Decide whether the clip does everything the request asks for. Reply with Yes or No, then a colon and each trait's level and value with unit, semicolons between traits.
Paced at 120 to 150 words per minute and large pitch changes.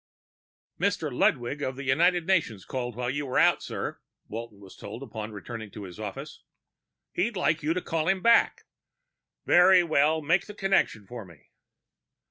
No: average, 165 wpm; wide, 7.6 semitones